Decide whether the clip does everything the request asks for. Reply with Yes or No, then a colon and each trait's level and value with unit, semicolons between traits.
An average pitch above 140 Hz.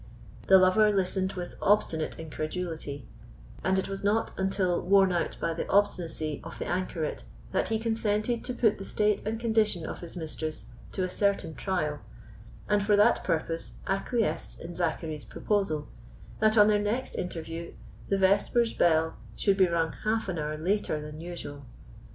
Yes: medium, 185 Hz